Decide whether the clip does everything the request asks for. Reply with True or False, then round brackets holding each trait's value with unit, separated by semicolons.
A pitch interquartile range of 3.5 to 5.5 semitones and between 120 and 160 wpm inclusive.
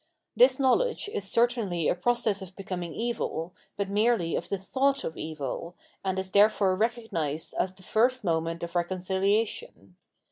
True (4.8 semitones; 155 wpm)